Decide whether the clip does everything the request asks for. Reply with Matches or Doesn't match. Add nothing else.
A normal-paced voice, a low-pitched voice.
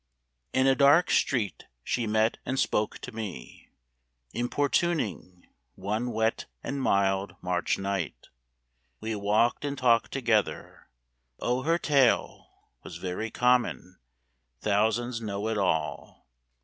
Doesn't match